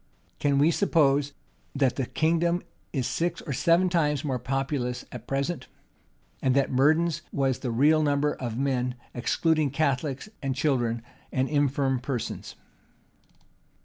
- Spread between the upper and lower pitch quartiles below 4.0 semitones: Yes, average, 3.0 semitones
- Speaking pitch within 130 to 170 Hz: Yes, medium, 140 Hz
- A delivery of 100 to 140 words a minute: Yes, slow, 135 wpm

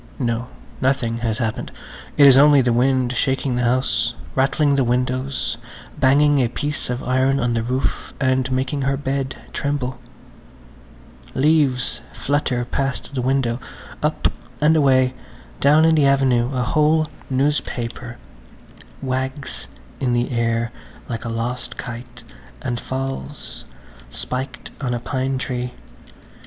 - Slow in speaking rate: Yes, slow, 130 wpm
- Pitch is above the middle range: No, low, 130 Hz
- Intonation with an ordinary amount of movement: No, narrow, 2.0 semitones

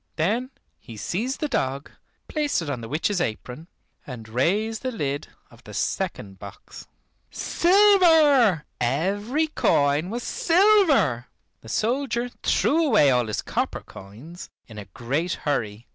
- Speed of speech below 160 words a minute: Yes, slow, 135 wpm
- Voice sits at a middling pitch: Yes, medium, 175 Hz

